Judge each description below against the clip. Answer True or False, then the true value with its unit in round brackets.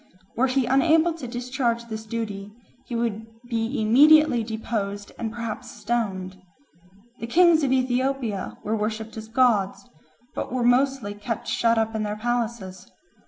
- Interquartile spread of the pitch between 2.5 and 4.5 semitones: True (2.9 semitones)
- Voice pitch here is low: False (230 Hz)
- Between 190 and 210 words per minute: False (145 wpm)